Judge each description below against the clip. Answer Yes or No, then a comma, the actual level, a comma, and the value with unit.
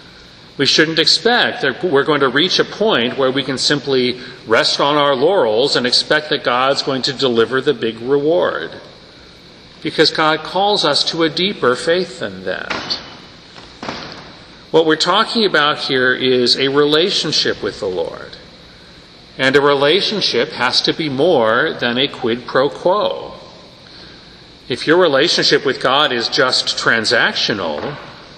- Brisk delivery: No, average, 145 wpm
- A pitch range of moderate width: No, wide, 7.7 semitones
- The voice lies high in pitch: No, medium, 155 Hz